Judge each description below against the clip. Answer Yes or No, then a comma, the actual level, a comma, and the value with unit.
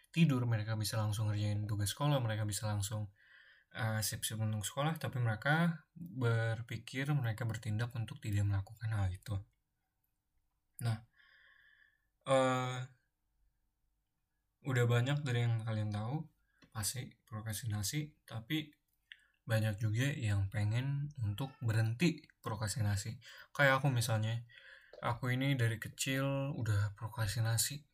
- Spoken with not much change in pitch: No, average, 3.7 semitones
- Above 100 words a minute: Yes, average, 110 wpm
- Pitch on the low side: Yes, low, 115 Hz